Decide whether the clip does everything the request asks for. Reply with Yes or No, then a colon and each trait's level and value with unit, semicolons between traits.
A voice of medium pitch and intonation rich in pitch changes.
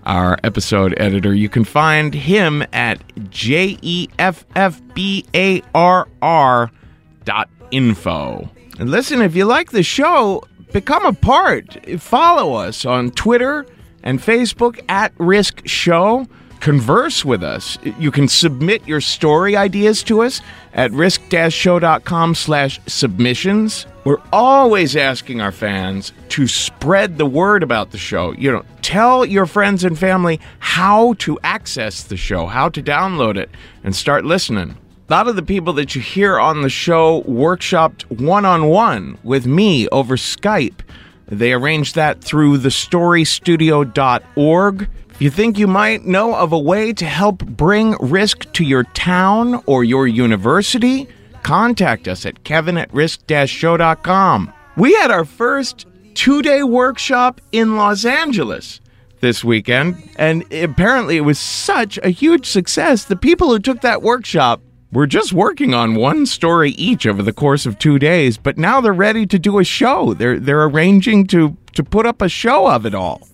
Yes: medium, 165 Hz; wide, 7.7 semitones